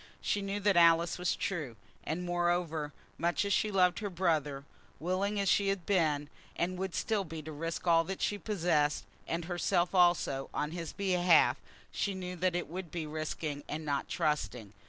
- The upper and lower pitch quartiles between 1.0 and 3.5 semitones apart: Yes, average, 3.2 semitones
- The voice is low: No, medium, 175 Hz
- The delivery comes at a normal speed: Yes, average, 180 wpm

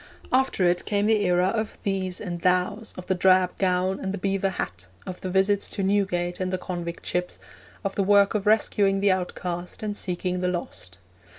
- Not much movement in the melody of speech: Yes, narrow, 1.9 semitones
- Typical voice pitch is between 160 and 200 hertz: Yes, medium, 185 Hz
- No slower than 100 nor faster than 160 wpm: No, average, 195 wpm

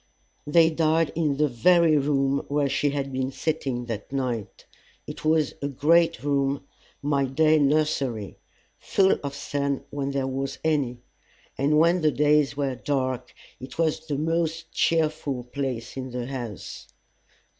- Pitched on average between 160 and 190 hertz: No, medium, 140 Hz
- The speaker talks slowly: No, average, 145 wpm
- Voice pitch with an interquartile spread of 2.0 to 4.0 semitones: Yes, average, 2.7 semitones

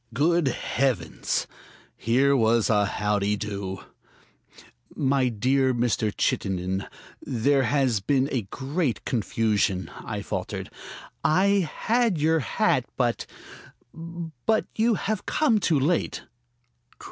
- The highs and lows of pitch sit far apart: Yes, wide, 7.2 semitones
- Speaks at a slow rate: Yes, slow, 105 wpm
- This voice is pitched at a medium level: No, low, 130 Hz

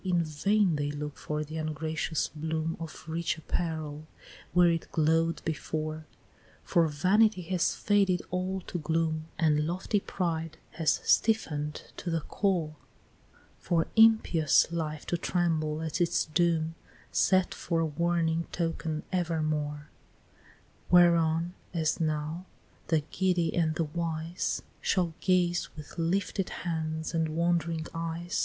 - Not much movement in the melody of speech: Yes, narrow, 1.9 semitones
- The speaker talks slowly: Yes, slow, 125 wpm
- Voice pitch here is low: No, medium, 165 Hz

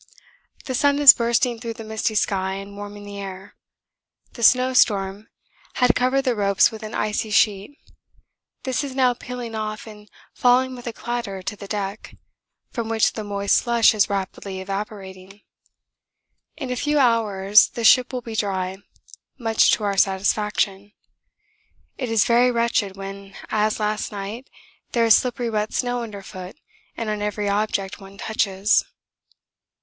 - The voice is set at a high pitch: Yes, high, 215 Hz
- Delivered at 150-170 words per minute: Yes, average, 155 wpm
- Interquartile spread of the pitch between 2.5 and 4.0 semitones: Yes, average, 3.2 semitones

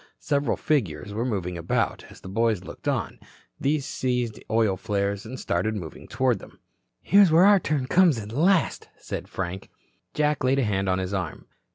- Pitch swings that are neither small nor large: No, wide, 6.7 semitones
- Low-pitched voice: Yes, low, 115 Hz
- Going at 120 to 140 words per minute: No, average, 180 wpm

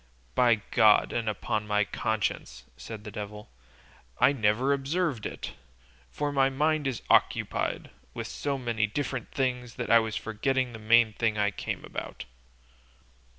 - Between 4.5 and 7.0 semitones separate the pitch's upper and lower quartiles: No, average, 4.0 semitones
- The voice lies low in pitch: Yes, low, 115 Hz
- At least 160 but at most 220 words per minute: No, average, 150 wpm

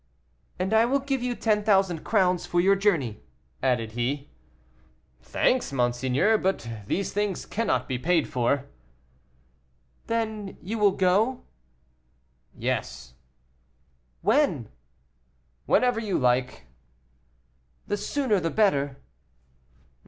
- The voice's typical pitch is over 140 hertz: Yes, high, 190 Hz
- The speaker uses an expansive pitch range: Yes, wide, 8.4 semitones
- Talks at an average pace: No, slow, 105 wpm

